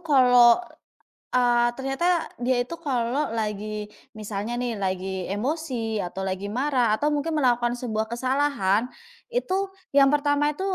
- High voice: Yes, high, 245 Hz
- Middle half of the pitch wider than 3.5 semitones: Yes, average, 5.0 semitones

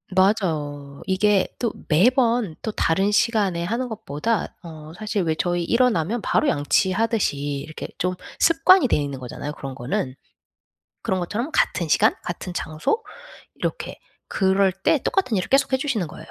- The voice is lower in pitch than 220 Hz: Yes, high, 190 Hz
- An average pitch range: No, wide, 6.5 semitones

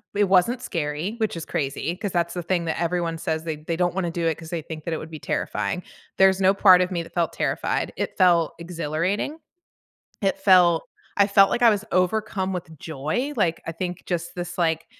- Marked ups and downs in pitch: No, narrow, 2.6 semitones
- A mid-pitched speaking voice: Yes, medium, 175 Hz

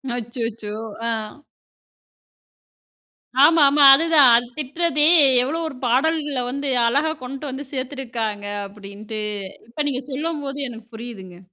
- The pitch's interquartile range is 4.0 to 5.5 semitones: Yes, average, 4.4 semitones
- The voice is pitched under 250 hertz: No, very high, 260 Hz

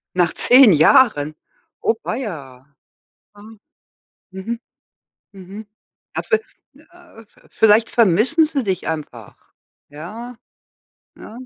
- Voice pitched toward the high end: Yes, high, 210 Hz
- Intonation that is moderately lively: No, wide, 6.0 semitones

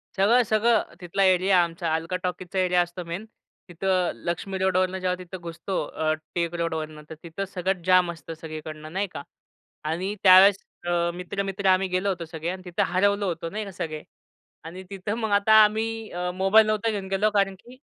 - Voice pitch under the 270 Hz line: Yes, medium, 185 Hz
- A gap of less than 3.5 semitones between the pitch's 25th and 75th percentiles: Yes, narrow, 2.6 semitones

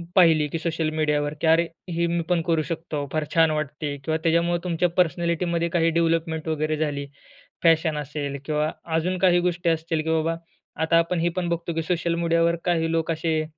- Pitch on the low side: No, medium, 165 Hz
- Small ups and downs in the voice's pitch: Yes, narrow, 1.4 semitones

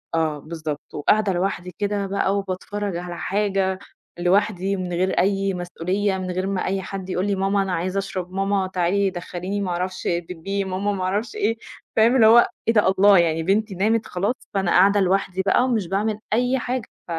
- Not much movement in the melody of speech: Yes, narrow, 1.9 semitones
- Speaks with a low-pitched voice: No, high, 195 Hz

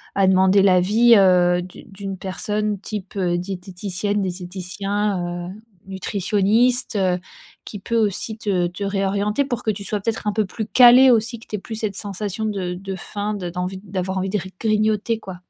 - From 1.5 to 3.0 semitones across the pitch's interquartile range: Yes, narrow, 2.4 semitones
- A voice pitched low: No, high, 200 Hz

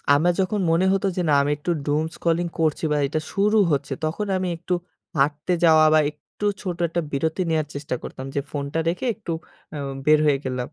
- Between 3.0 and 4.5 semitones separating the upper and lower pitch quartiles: Yes, average, 3.3 semitones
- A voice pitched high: No, medium, 155 Hz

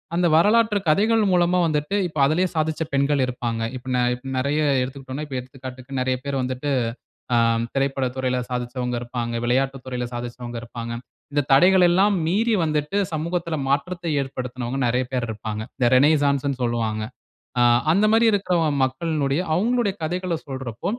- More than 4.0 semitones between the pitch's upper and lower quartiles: Yes, average, 5.2 semitones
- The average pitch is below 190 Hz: Yes, low, 135 Hz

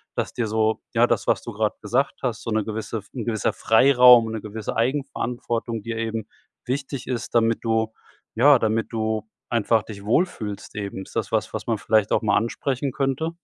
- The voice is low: Yes, low, 115 Hz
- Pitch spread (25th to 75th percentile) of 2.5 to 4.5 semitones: No, narrow, 2.1 semitones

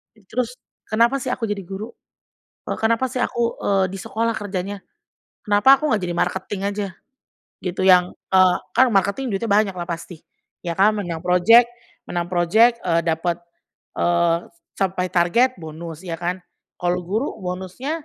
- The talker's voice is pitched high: Yes, high, 195 Hz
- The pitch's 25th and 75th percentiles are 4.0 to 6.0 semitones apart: Yes, average, 4.3 semitones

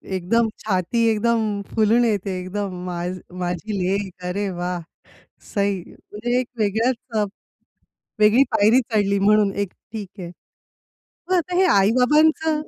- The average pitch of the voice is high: Yes, high, 210 Hz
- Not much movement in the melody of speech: No, average, 3.3 semitones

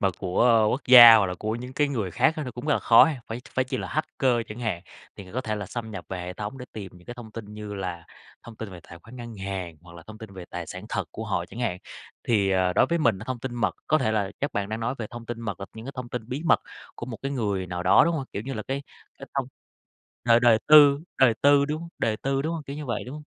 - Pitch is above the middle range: No, low, 115 Hz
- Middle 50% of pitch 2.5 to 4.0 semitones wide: No, average, 4.7 semitones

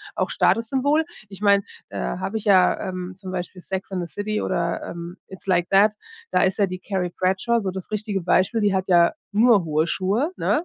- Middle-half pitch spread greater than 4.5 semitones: No, average, 2.7 semitones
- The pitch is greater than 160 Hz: Yes, high, 190 Hz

